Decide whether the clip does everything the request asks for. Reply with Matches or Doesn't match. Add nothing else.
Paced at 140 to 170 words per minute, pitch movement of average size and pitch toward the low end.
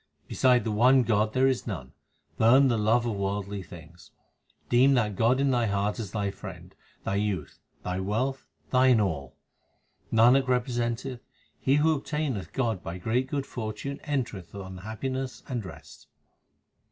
Matches